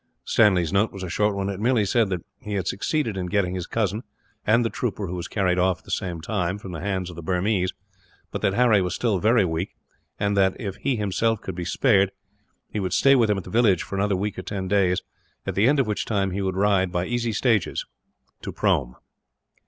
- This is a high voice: No, low, 100 Hz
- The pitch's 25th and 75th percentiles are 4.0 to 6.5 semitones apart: No, average, 2.8 semitones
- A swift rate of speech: Yes, fast, 235 wpm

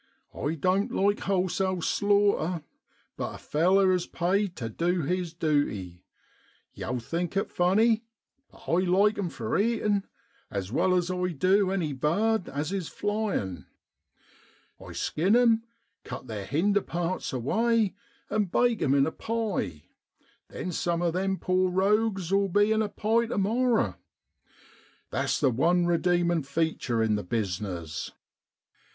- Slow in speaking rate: No, average, 145 wpm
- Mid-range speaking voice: Yes, medium, 180 Hz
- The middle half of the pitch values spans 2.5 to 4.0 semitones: No, average, 5.2 semitones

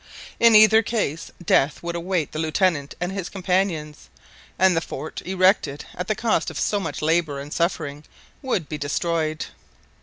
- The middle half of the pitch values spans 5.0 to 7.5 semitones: No, average, 3.9 semitones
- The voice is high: No, medium, 170 Hz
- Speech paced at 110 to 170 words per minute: Yes, average, 160 wpm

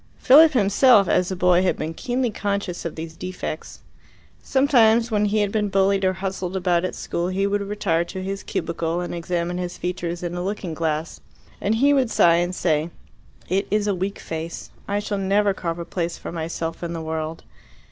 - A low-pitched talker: No, medium, 185 Hz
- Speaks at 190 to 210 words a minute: Yes, average, 200 wpm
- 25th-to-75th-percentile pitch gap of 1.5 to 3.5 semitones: Yes, average, 3.2 semitones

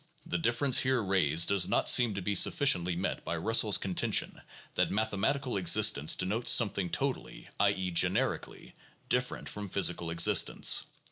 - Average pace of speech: Yes, average, 150 wpm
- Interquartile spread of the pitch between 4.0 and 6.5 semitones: Yes, average, 4.9 semitones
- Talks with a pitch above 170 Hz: No, low, 100 Hz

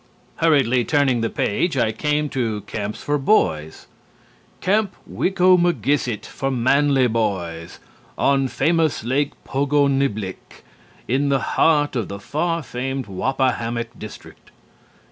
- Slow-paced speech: Yes, slow, 110 wpm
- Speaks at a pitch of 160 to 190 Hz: No, low, 135 Hz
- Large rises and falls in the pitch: No, average, 4.4 semitones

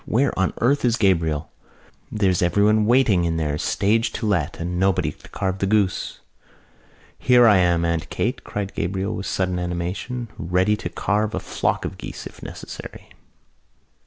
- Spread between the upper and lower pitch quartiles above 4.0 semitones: No, average, 3.6 semitones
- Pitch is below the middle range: Yes, very low, 95 Hz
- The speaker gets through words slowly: No, average, 160 wpm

